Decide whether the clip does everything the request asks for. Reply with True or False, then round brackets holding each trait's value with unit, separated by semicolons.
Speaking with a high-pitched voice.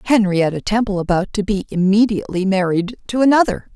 True (200 Hz)